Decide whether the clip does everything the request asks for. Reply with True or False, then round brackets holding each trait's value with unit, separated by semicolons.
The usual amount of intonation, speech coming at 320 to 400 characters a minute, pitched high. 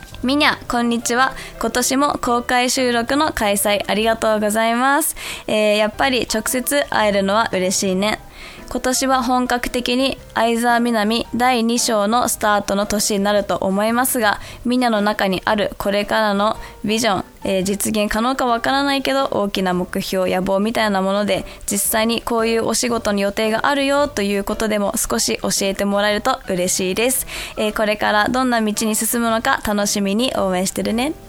True (3.3 semitones; 355 characters per minute; 220 Hz)